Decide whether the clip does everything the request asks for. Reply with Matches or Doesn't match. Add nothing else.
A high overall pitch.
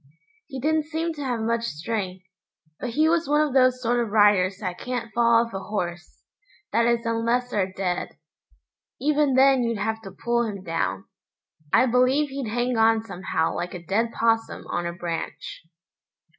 Matches